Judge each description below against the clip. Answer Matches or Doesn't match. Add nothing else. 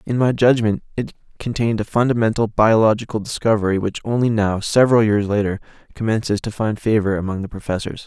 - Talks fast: Doesn't match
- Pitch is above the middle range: Doesn't match